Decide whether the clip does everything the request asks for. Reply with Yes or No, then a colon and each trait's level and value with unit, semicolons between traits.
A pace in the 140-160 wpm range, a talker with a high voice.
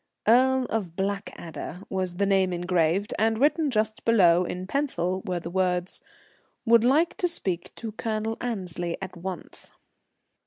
Yes: average, 145 wpm; high, 195 Hz